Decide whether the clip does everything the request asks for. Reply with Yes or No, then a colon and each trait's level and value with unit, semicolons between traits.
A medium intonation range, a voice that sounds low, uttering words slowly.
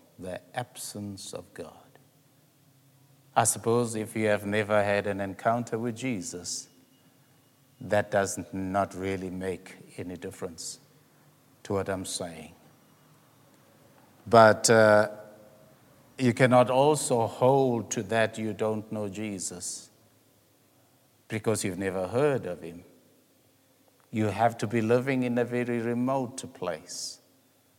Yes: average, 4.3 semitones; low, 115 Hz; slow, 115 wpm